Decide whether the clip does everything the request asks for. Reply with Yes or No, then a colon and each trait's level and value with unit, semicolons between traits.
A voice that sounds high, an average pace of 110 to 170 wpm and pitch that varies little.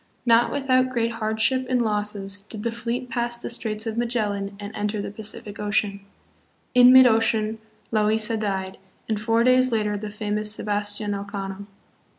Yes: high, 215 Hz; average, 160 wpm; narrow, 2.2 semitones